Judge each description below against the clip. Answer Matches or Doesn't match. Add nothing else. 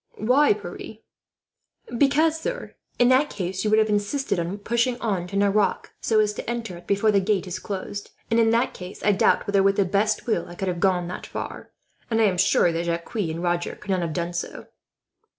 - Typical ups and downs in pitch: Matches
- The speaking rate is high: Matches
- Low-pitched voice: Doesn't match